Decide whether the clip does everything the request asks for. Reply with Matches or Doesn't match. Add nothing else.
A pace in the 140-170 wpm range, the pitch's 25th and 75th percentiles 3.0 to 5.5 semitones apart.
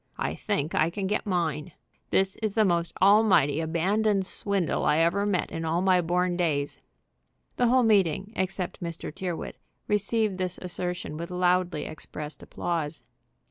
Matches